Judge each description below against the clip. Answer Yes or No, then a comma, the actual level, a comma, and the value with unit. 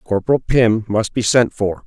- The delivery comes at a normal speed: Yes, average, 195 wpm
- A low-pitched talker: Yes, low, 115 Hz